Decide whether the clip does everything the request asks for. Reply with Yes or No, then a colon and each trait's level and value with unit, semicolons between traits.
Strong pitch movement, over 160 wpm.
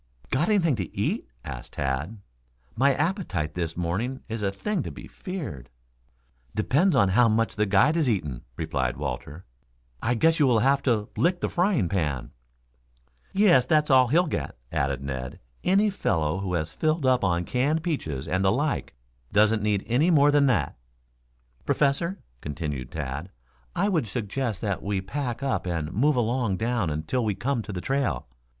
Yes: wide, 8.6 semitones; average, 170 wpm